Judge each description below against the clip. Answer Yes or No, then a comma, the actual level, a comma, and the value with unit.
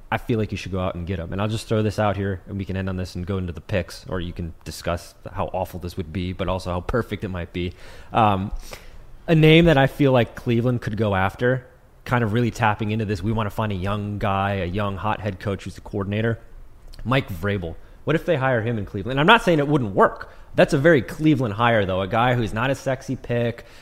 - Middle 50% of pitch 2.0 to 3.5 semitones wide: No, average, 4.3 semitones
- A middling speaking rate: No, fast, 265 wpm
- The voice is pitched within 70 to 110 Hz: Yes, low, 105 Hz